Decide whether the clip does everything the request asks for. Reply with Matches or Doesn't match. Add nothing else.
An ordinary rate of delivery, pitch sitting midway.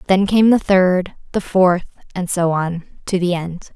Matches